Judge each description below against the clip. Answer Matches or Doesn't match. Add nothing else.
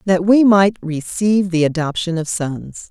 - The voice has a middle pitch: Matches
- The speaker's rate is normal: Matches